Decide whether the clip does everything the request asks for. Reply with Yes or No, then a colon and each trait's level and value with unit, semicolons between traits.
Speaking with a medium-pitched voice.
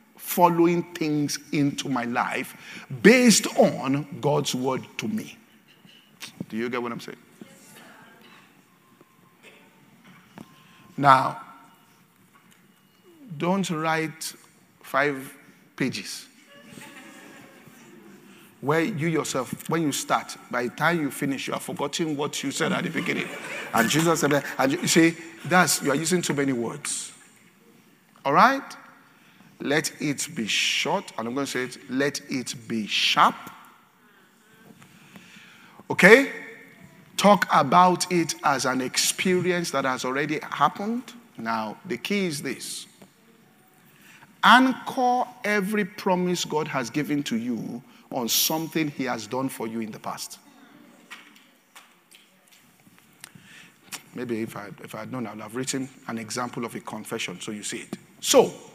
Yes: medium, 165 Hz